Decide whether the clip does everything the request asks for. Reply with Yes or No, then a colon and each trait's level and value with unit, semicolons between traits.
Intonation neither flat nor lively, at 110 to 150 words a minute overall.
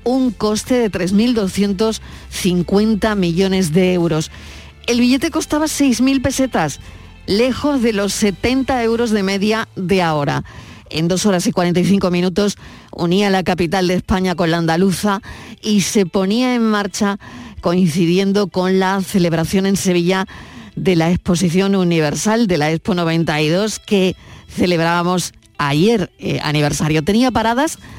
Yes: average, 3.7 semitones; average, 130 wpm